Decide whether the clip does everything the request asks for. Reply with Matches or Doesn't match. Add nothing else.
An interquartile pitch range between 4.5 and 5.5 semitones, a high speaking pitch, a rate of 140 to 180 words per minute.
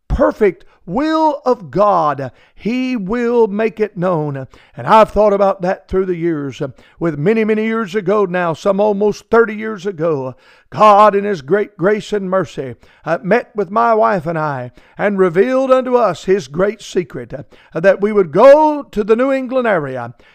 Matches